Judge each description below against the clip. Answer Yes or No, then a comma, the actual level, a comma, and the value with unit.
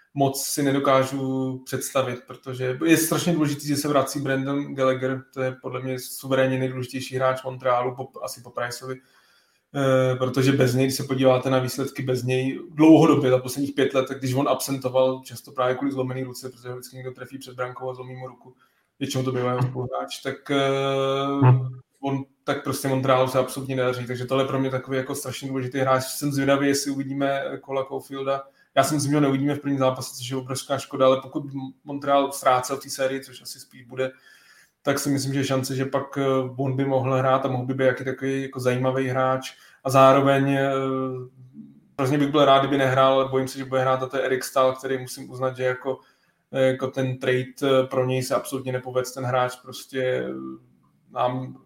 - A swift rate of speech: Yes, fast, 195 wpm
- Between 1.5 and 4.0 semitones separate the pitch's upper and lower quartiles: No, narrow, 0.9 semitones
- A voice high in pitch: No, low, 130 Hz